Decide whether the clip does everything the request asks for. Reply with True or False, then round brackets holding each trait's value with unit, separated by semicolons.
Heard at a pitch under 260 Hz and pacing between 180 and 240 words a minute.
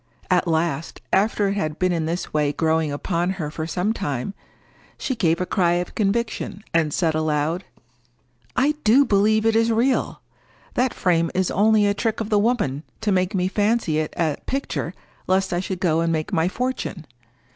True (185 Hz; 185 wpm)